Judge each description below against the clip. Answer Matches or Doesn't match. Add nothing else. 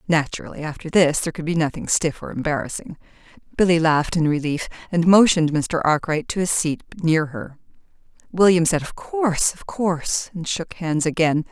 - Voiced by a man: Doesn't match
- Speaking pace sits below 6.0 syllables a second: Matches